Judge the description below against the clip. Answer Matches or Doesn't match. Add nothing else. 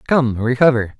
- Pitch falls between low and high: Doesn't match